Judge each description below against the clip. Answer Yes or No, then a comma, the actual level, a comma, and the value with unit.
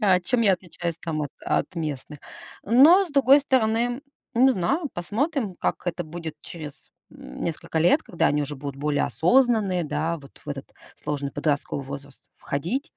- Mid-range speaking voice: Yes, medium, 175 Hz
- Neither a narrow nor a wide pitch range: No, wide, 8.4 semitones